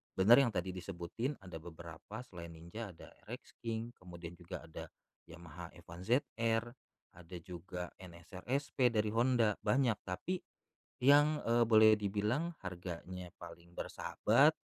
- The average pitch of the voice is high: No, very low, 95 Hz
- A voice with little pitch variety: No, average, 5.1 semitones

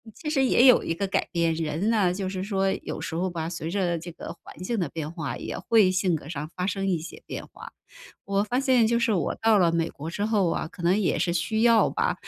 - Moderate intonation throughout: Yes, average, 4.3 semitones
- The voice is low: No, medium, 185 Hz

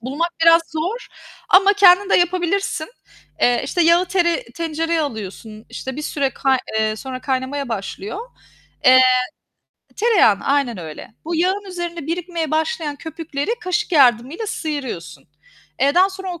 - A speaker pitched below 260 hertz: No, very high, 315 Hz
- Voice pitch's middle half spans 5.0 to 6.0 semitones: Yes, wide, 5.4 semitones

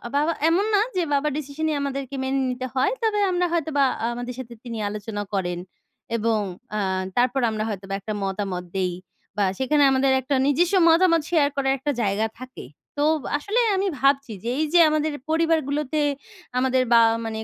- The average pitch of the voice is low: No, very high, 270 Hz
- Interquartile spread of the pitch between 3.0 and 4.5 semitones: No, average, 5.2 semitones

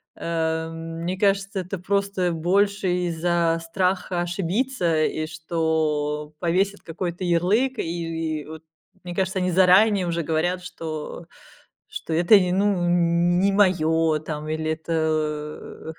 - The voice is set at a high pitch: No, medium, 170 Hz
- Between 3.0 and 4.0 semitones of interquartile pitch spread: No, narrow, 2.6 semitones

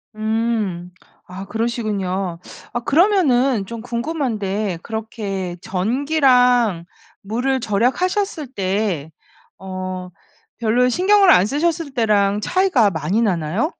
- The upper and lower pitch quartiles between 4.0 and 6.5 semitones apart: Yes, wide, 5.4 semitones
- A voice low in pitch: No, high, 220 Hz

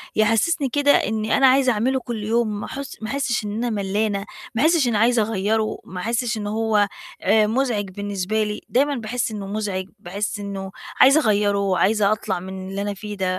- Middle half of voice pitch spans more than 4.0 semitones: No, average, 2.9 semitones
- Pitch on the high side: Yes, high, 215 Hz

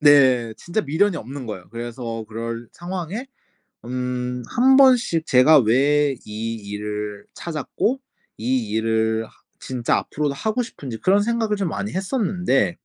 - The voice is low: Yes, low, 130 Hz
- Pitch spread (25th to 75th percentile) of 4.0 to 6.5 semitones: No, wide, 8.2 semitones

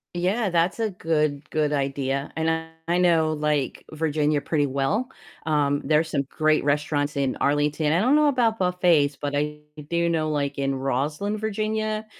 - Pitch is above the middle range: No, medium, 155 Hz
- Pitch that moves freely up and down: No, average, 3.7 semitones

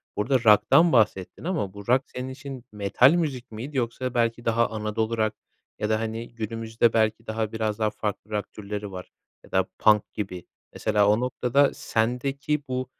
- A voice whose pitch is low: Yes, low, 115 Hz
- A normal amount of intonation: Yes, average, 3.1 semitones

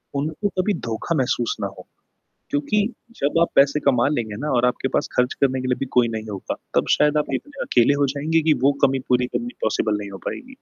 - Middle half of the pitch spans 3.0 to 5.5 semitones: Yes, average, 3.8 semitones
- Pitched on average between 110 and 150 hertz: Yes, low, 135 Hz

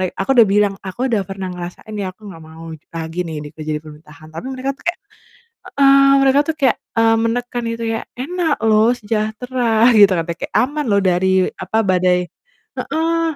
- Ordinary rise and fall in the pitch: No, wide, 5.9 semitones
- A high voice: Yes, high, 215 Hz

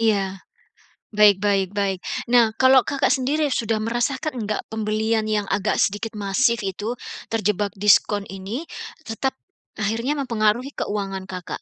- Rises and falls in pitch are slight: No, average, 3.0 semitones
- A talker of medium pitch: No, high, 215 Hz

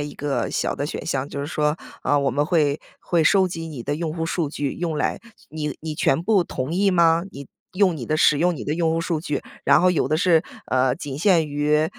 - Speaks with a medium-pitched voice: Yes, medium, 155 Hz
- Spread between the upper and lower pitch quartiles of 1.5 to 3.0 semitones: Yes, average, 2.7 semitones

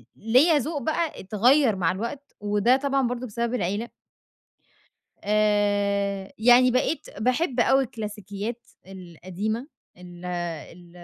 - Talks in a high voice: Yes, high, 215 Hz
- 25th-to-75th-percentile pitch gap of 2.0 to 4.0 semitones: No, average, 4.4 semitones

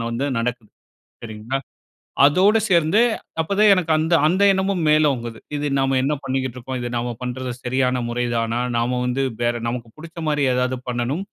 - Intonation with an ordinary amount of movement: Yes, average, 4.3 semitones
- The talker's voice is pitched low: Yes, low, 130 Hz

